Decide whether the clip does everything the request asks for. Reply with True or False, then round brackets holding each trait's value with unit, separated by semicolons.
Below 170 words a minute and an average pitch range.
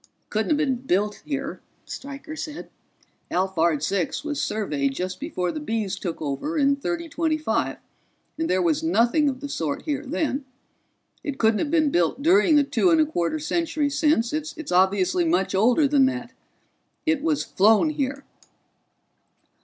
False (160 wpm; 8.2 semitones)